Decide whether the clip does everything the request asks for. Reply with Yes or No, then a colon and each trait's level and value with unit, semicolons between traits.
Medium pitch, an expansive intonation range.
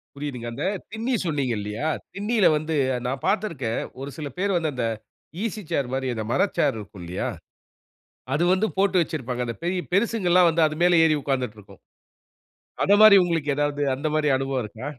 Yes: medium, 150 Hz; wide, 6.2 semitones